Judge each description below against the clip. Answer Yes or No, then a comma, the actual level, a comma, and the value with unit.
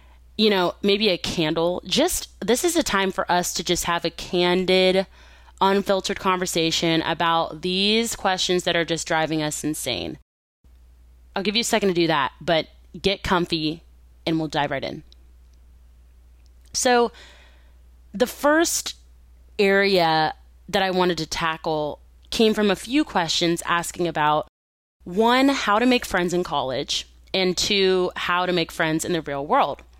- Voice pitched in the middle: Yes, medium, 170 Hz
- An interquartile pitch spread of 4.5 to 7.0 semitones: Yes, average, 5.2 semitones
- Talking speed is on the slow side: No, average, 155 wpm